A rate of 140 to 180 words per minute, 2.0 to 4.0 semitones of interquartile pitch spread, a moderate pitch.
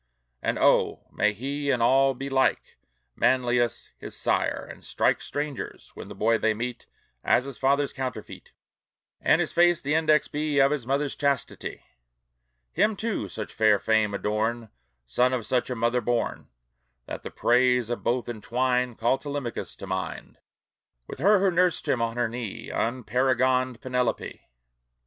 No: average, 155 wpm; average, 3.0 semitones; low, 125 Hz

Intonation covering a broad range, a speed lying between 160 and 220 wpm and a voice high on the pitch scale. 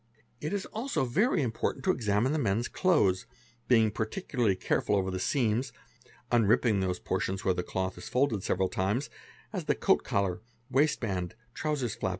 No: wide, 6.3 semitones; average, 170 wpm; low, 110 Hz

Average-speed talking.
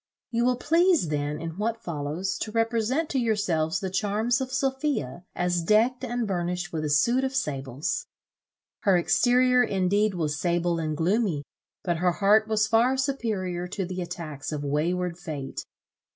Yes: average, 160 wpm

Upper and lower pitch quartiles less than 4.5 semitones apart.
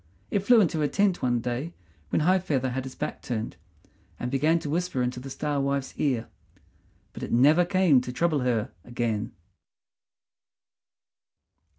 No: average, 5.3 semitones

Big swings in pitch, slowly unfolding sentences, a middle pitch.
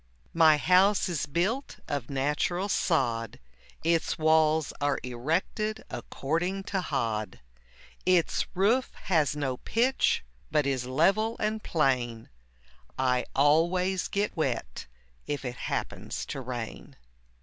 Yes: wide, 6.0 semitones; slow, 115 wpm; medium, 155 Hz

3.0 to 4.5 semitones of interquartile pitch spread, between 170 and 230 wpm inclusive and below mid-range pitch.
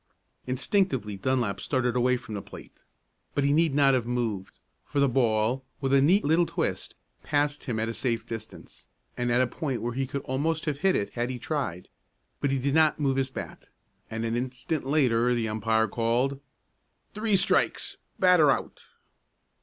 Yes: average, 3.8 semitones; average, 180 wpm; low, 130 Hz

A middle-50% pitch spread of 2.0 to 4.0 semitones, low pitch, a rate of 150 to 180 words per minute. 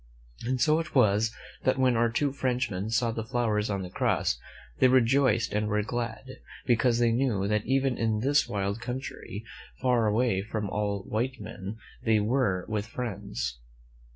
Yes: average, 3.3 semitones; low, 115 Hz; average, 170 wpm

